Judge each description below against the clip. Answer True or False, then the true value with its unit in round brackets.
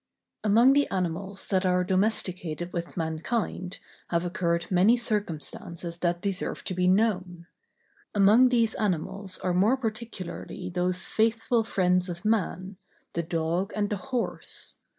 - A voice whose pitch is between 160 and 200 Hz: True (185 Hz)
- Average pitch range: True (3.6 semitones)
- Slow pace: True (130 wpm)